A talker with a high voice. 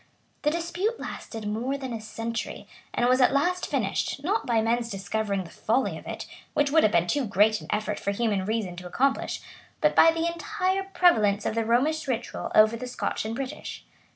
Yes: high, 235 Hz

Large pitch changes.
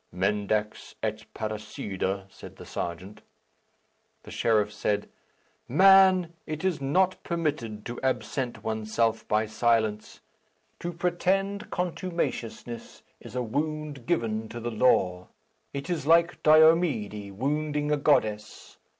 Yes: wide, 6.8 semitones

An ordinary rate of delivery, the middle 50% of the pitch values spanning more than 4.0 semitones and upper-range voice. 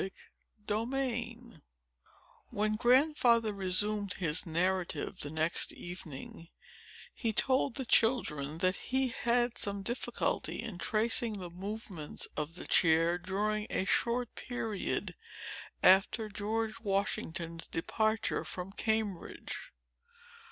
No: slow, 105 wpm; average, 4.6 semitones; high, 210 Hz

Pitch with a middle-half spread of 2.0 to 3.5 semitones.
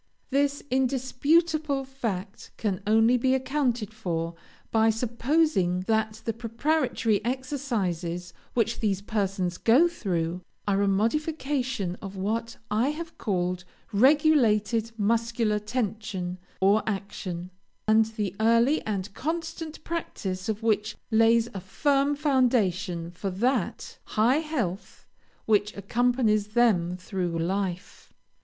No: average, 5.1 semitones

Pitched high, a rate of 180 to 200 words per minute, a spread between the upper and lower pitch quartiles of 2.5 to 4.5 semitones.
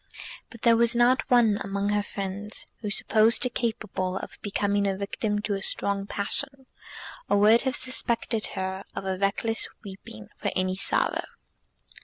No: high, 205 Hz; average, 155 wpm; average, 2.8 semitones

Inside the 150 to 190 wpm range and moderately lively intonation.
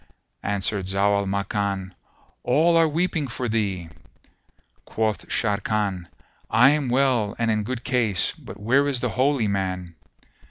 No: slow, 135 wpm; average, 4.5 semitones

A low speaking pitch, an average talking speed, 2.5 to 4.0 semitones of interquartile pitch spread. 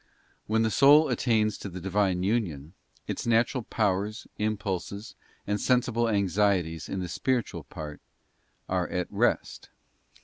No: low, 105 Hz; slow, 130 wpm; average, 3.7 semitones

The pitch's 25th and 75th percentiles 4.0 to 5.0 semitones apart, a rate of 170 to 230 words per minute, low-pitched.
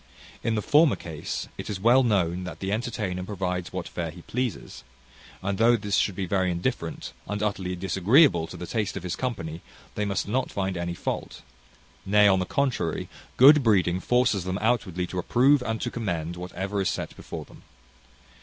Yes: average, 4.3 semitones; average, 185 wpm; low, 100 Hz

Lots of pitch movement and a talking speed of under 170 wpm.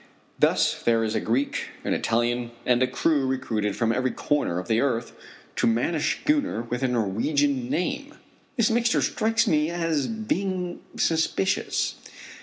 Yes: wide, 6.9 semitones; average, 155 wpm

